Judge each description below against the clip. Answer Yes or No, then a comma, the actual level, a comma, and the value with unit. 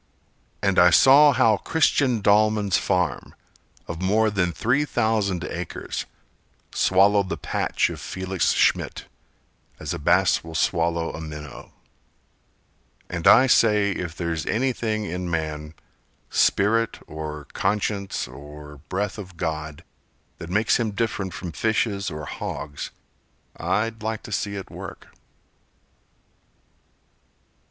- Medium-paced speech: No, slow, 120 wpm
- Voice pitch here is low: Yes, very low, 95 Hz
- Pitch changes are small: No, average, 4.6 semitones